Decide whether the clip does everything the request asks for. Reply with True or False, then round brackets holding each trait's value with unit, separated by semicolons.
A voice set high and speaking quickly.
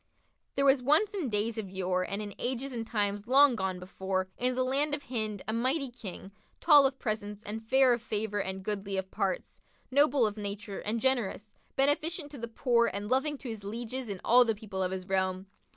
True (225 Hz; 215 wpm)